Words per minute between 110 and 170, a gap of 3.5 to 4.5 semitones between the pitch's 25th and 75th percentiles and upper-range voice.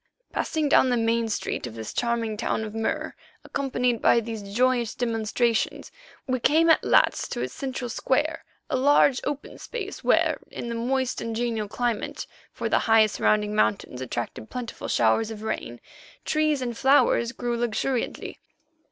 No: average, 160 wpm; average, 2.9 semitones; high, 235 Hz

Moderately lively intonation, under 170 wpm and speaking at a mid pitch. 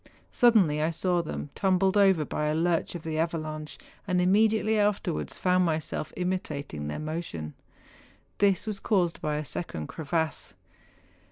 Yes: average, 3.8 semitones; average, 145 wpm; medium, 170 Hz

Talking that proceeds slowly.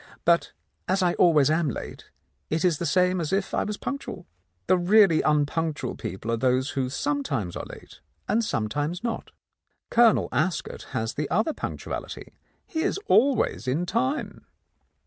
No: average, 165 wpm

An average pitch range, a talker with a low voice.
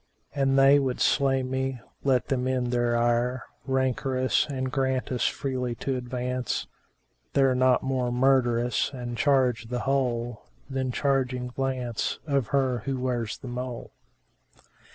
No: narrow, 1.5 semitones; low, 130 Hz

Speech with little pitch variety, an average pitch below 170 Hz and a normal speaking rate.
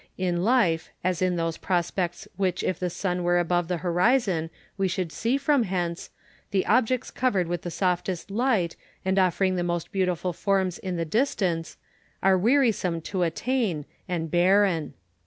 No: narrow, 2.3 semitones; medium, 180 Hz; average, 165 wpm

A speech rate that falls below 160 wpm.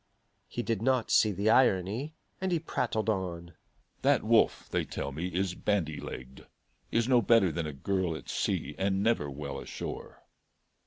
No: average, 165 wpm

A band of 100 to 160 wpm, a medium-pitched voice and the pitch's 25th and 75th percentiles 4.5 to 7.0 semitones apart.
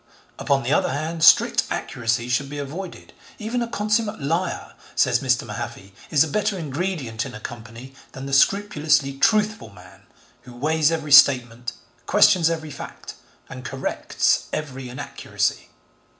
Yes: average, 145 wpm; medium, 145 Hz; average, 5.1 semitones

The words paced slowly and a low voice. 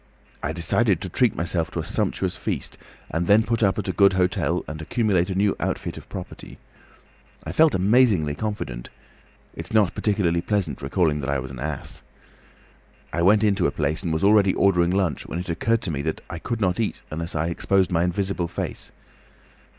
No: average, 195 wpm; very low, 90 Hz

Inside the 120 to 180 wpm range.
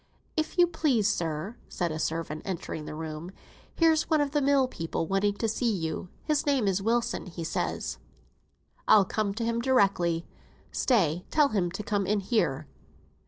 Yes: average, 170 wpm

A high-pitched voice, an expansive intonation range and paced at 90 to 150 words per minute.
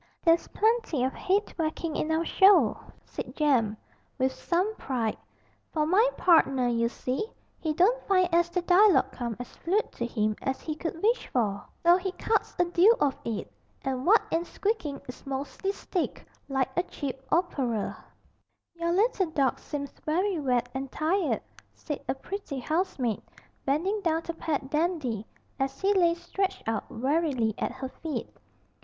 No: very high, 320 Hz; wide, 5.7 semitones; average, 160 wpm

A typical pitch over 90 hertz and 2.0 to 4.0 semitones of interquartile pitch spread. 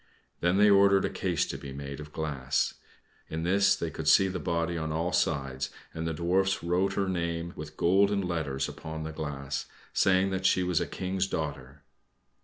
No: very low, 85 Hz; average, 3.6 semitones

